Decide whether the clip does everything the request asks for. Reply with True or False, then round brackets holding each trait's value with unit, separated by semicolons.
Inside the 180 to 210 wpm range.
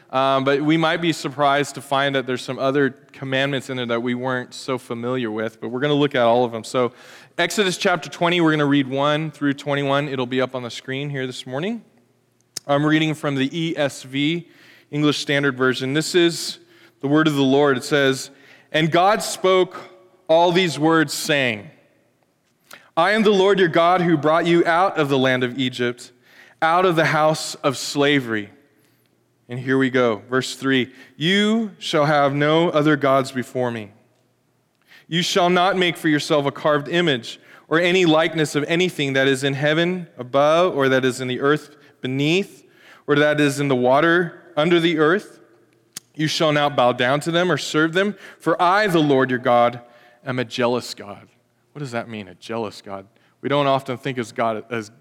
True (195 wpm)